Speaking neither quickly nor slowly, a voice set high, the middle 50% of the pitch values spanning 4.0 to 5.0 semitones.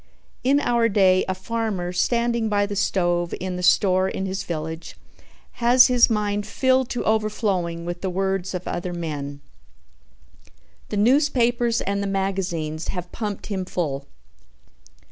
Yes: average, 145 wpm; high, 195 Hz; average, 4.3 semitones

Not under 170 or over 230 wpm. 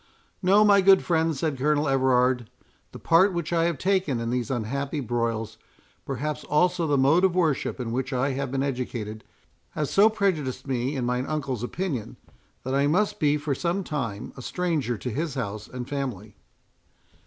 Yes: average, 175 wpm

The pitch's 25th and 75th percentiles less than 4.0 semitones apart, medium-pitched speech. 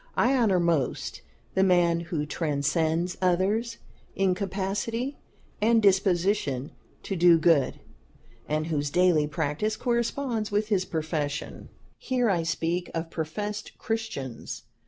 No: average, 4.8 semitones; medium, 180 Hz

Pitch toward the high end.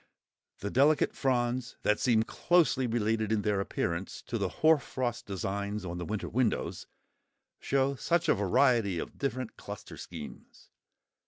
No: low, 115 Hz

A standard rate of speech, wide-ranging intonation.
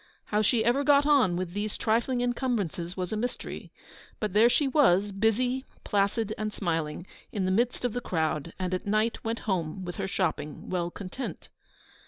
No: average, 180 wpm; average, 4.9 semitones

